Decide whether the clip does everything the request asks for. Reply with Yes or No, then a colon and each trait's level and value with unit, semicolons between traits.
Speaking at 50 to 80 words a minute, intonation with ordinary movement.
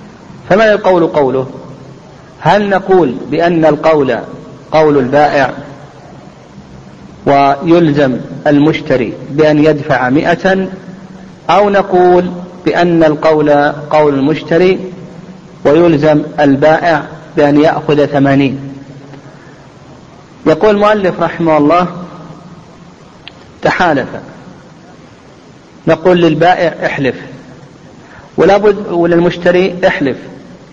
Yes: average, 70 wpm; average, 3.5 semitones